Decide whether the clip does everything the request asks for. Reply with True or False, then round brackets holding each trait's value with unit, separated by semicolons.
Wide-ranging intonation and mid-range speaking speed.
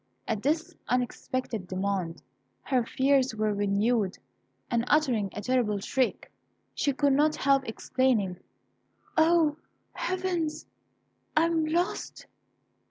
False (6.3 semitones; 105 wpm)